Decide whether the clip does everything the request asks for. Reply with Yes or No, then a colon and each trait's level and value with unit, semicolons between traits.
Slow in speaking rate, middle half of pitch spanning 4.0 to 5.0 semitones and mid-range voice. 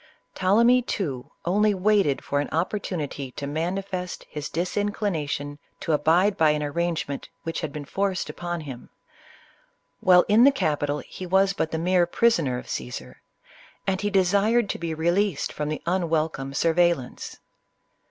No: average, 155 wpm; average, 4.7 semitones; medium, 170 Hz